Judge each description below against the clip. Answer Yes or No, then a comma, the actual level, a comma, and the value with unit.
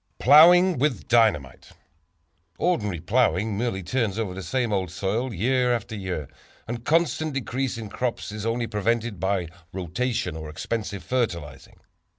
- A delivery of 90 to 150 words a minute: Yes, average, 140 wpm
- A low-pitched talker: Yes, low, 110 Hz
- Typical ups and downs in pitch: Yes, average, 4.8 semitones